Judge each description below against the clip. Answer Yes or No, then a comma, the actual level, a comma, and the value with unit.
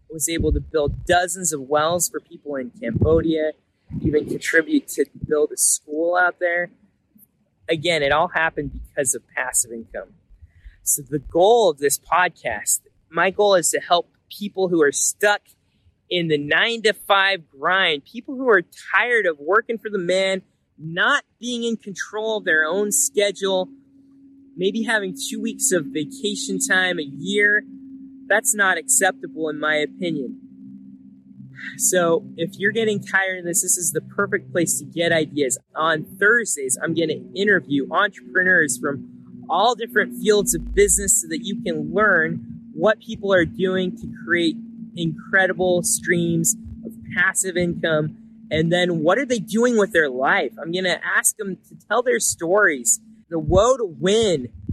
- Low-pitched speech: No, medium, 185 Hz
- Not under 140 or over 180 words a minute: Yes, average, 160 wpm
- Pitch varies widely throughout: Yes, wide, 5.8 semitones